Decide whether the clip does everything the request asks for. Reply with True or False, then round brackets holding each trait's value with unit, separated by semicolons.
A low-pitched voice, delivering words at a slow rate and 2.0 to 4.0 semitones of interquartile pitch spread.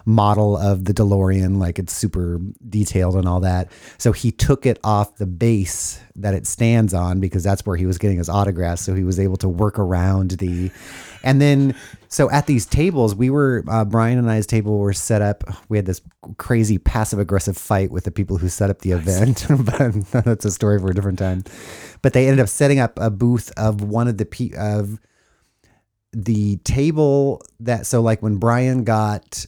False (105 Hz; 200 wpm; 3.4 semitones)